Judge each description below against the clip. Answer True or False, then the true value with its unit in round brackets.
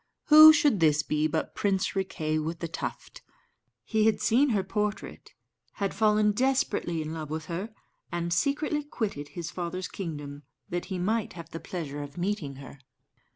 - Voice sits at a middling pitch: True (180 Hz)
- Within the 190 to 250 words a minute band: False (165 wpm)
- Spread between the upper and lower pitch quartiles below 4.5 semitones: False (5.4 semitones)